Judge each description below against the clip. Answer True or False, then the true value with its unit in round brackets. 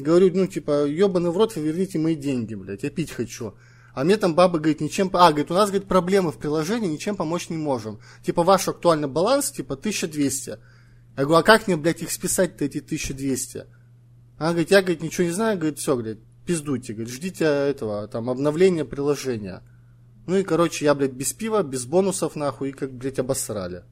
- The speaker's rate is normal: False (200 wpm)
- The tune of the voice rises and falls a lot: True (5.9 semitones)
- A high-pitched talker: False (150 Hz)